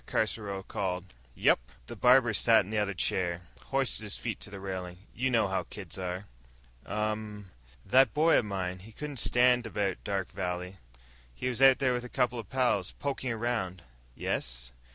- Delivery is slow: No, average, 180 wpm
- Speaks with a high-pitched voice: No, low, 105 Hz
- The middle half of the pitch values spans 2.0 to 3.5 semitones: No, average, 4.7 semitones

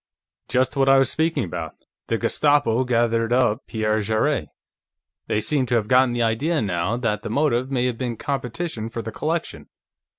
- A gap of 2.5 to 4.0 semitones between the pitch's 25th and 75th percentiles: Yes, average, 3.3 semitones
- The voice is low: Yes, low, 120 Hz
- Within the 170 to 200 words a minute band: Yes, average, 175 wpm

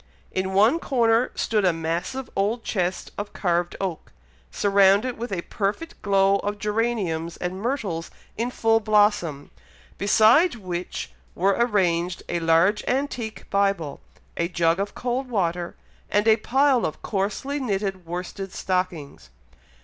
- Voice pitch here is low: No, high, 200 Hz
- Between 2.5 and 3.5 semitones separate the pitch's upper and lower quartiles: No, average, 4.2 semitones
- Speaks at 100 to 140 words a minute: Yes, slow, 135 wpm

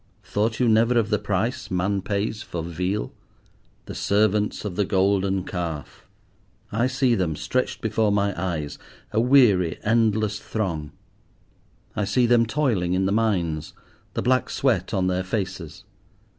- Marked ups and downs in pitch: No, average, 3.5 semitones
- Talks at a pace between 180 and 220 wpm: No, average, 145 wpm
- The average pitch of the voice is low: Yes, low, 100 Hz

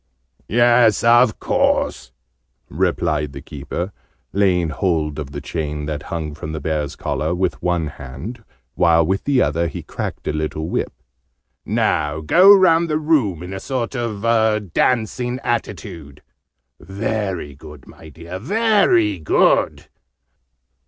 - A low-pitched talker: Yes, very low, 90 Hz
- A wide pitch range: Yes, wide, 7.1 semitones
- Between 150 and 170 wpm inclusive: No, slow, 135 wpm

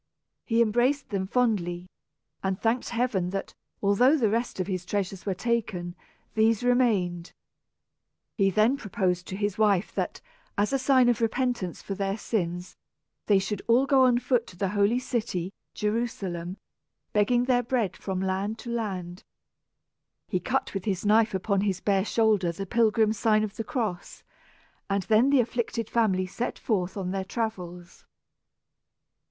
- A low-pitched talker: No, high, 210 Hz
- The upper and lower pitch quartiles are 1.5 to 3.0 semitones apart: No, average, 3.8 semitones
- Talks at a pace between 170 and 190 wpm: No, average, 160 wpm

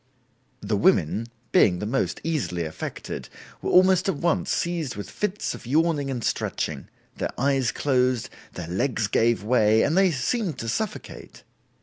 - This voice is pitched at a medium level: No, low, 130 Hz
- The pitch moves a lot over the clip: Yes, wide, 7.0 semitones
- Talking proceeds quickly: No, average, 150 wpm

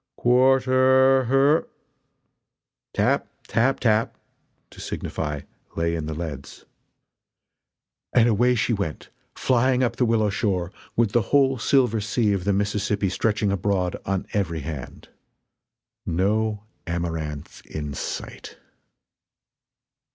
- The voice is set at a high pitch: No, low, 105 Hz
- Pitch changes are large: Yes, wide, 6.0 semitones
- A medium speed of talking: No, slow, 115 wpm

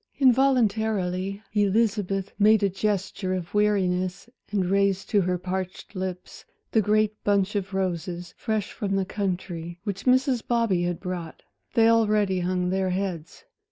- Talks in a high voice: Yes, high, 195 Hz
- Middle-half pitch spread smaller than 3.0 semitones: Yes, narrow, 2.6 semitones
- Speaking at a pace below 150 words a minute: Yes, average, 140 wpm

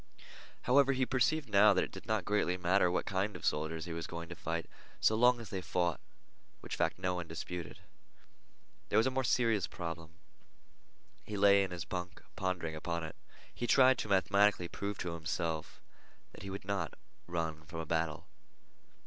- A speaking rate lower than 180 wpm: No, average, 185 wpm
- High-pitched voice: No, very low, 90 Hz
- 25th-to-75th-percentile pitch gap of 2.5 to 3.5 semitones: No, average, 3.9 semitones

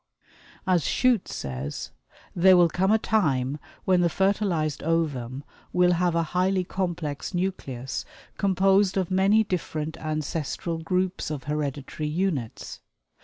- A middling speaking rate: No, slow, 120 wpm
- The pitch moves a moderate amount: Yes, average, 3.9 semitones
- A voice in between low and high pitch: Yes, medium, 175 Hz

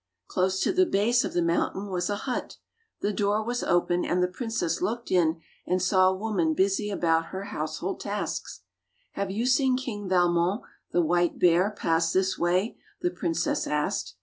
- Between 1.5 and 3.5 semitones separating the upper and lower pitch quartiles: Yes, average, 3.1 semitones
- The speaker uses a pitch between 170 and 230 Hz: Yes, medium, 185 Hz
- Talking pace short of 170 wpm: No, average, 175 wpm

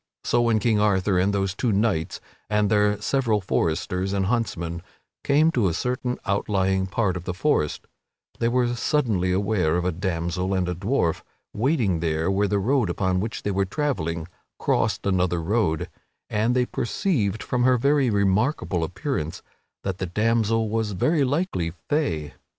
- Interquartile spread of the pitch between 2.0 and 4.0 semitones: No, average, 4.5 semitones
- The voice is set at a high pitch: No, low, 100 Hz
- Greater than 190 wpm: No, average, 160 wpm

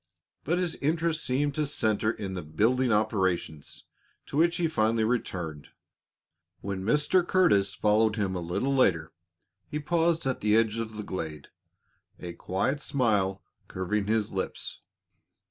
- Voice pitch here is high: No, low, 110 Hz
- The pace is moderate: Yes, average, 145 wpm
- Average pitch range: No, wide, 7.0 semitones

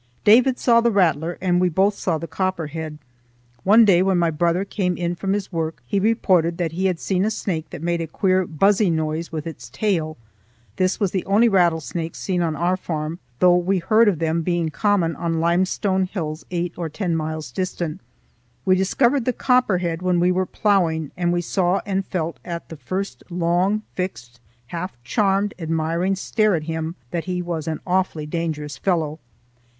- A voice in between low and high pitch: Yes, medium, 175 Hz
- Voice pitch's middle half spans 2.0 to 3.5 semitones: Yes, average, 2.8 semitones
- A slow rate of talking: No, average, 185 wpm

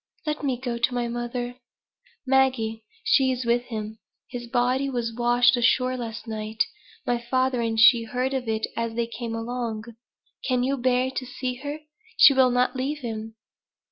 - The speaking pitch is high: Yes, high, 245 Hz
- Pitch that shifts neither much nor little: No, narrow, 1.9 semitones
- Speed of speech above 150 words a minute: Yes, average, 170 wpm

